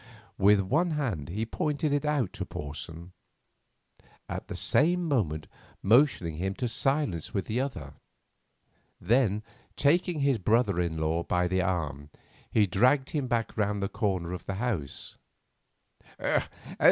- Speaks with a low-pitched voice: Yes, low, 105 Hz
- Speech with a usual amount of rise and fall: No, wide, 7.4 semitones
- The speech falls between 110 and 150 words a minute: Yes, average, 140 wpm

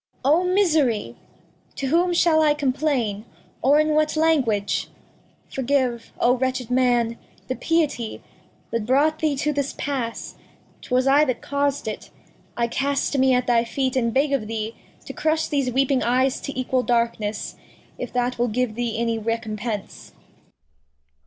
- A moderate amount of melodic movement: Yes, average, 3.5 semitones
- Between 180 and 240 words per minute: No, average, 155 wpm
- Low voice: No, very high, 255 Hz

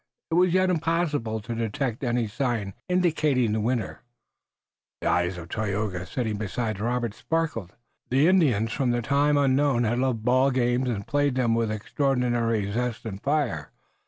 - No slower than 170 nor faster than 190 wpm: No, average, 160 wpm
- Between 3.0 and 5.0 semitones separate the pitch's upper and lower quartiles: Yes, average, 4.2 semitones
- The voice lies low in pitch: Yes, low, 120 Hz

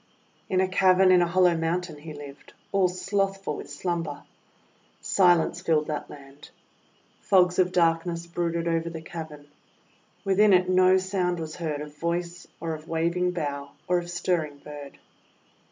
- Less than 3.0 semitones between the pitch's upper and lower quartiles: Yes, narrow, 2.5 semitones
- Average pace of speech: Yes, average, 155 wpm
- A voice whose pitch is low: No, medium, 170 Hz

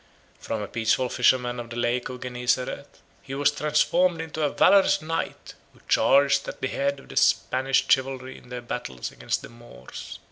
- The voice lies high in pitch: No, low, 130 Hz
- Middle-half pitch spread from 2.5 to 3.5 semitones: Yes, average, 3.0 semitones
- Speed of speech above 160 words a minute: Yes, average, 180 wpm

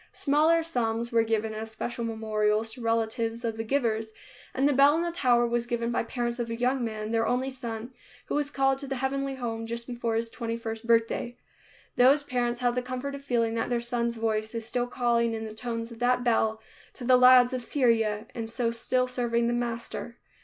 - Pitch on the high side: Yes, high, 235 Hz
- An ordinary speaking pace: No, fast, 215 wpm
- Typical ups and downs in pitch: No, narrow, 1.8 semitones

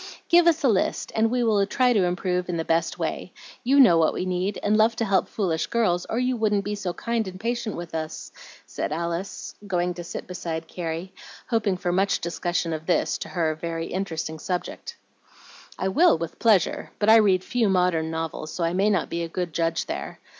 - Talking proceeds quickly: Yes, fast, 210 wpm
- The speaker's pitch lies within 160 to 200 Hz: Yes, medium, 185 Hz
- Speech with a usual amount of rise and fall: Yes, average, 4.3 semitones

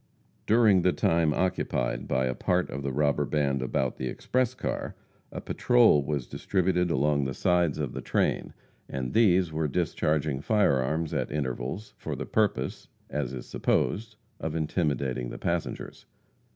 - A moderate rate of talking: Yes, average, 155 wpm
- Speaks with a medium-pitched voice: No, very low, 75 Hz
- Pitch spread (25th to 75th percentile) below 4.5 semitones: No, average, 5.0 semitones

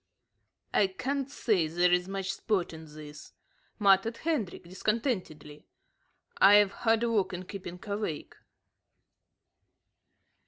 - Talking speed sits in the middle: No, slow, 95 wpm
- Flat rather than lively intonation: No, average, 4.0 semitones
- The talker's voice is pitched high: Yes, high, 195 Hz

